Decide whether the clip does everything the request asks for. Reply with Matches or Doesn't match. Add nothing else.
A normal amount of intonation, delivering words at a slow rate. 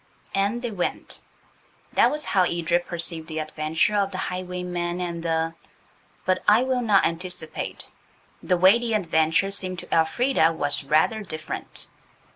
Doesn't match